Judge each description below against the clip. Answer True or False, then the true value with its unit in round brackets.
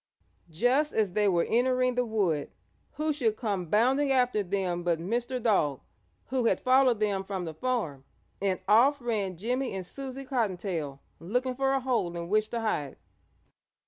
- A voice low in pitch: False (220 Hz)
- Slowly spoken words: False (165 wpm)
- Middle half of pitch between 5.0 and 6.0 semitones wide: True (5.6 semitones)